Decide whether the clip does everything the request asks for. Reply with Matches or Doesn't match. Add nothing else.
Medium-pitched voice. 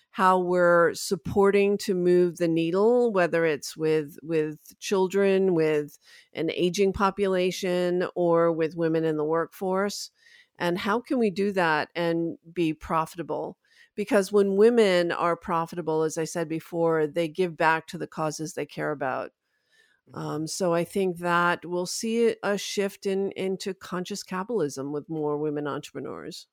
Matches